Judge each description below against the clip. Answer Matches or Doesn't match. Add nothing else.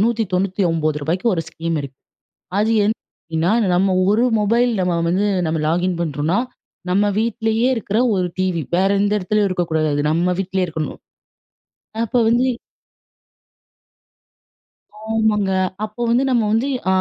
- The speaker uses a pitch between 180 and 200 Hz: Matches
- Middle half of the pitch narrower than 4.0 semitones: Doesn't match